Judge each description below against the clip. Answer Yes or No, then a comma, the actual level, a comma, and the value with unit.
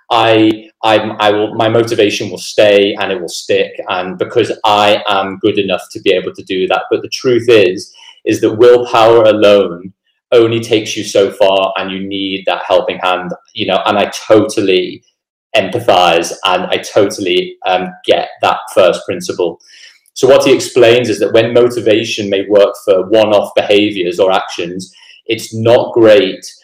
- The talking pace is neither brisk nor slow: Yes, average, 170 wpm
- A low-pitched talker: Yes, low, 115 Hz